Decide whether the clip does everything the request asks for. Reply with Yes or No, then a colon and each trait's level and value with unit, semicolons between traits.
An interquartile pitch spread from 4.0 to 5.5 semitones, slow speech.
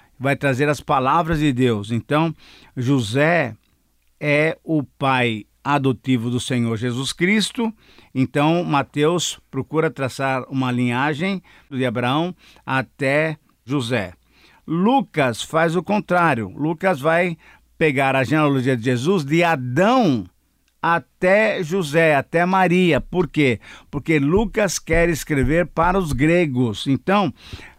Yes: average, 4.7 semitones; slow, 115 wpm